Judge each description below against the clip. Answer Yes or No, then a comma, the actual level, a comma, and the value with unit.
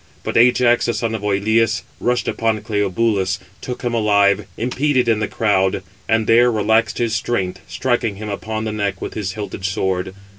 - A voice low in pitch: Yes, low, 110 Hz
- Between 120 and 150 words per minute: No, average, 175 wpm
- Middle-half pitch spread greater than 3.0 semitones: No, narrow, 2.6 semitones